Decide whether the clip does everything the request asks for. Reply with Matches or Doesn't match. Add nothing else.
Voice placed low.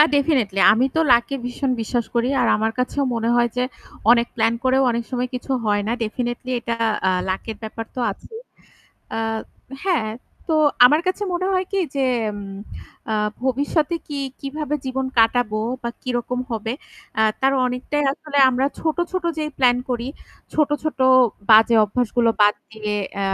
Doesn't match